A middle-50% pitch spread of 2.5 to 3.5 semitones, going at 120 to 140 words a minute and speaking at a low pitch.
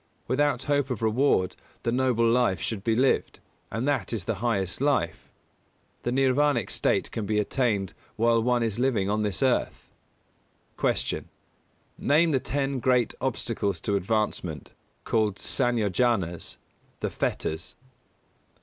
No: average, 4.3 semitones; slow, 135 wpm; low, 115 Hz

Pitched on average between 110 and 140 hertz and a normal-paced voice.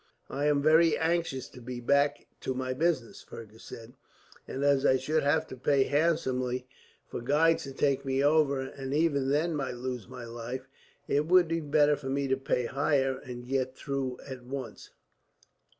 Yes: low, 135 Hz; average, 180 wpm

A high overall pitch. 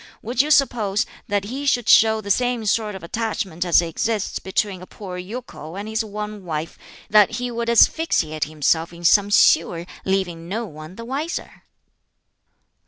Yes: high, 205 Hz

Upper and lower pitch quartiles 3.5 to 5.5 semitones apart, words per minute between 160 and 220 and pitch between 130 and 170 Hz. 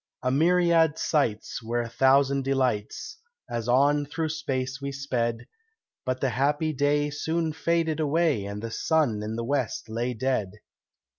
No: average, 4.5 semitones; average, 150 wpm; low, 135 Hz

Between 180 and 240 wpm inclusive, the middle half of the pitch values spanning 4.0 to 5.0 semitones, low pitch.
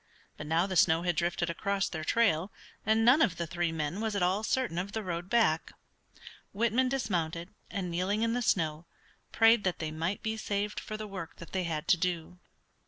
No: fast, 205 wpm; average, 4.4 semitones; medium, 185 Hz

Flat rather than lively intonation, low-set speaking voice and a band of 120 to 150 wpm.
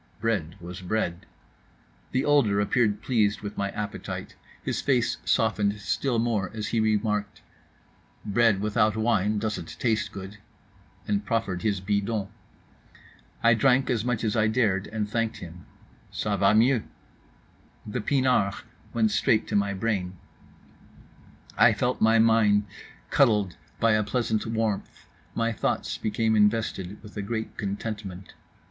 Yes: narrow, 2.0 semitones; low, 105 Hz; slow, 135 wpm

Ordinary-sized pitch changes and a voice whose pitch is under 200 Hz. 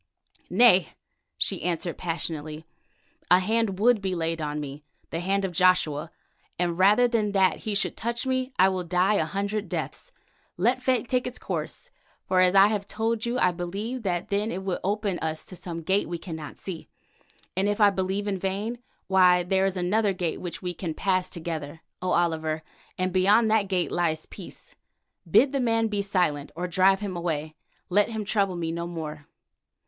Yes: average, 3.4 semitones; medium, 185 Hz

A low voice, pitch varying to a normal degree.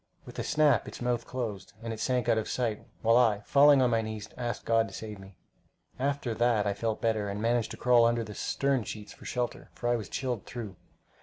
No: low, 115 Hz; narrow, 2.3 semitones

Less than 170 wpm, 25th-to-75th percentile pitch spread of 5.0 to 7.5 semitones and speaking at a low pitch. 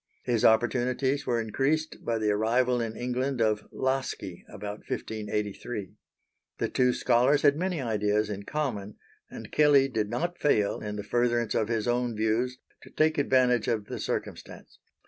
No: average, 155 wpm; average, 3.6 semitones; low, 120 Hz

